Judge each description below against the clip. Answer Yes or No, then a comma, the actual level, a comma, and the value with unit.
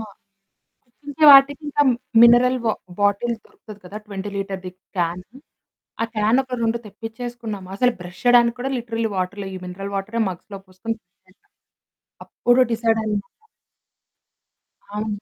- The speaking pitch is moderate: No, high, 220 Hz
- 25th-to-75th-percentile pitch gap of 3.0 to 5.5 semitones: Yes, average, 3.6 semitones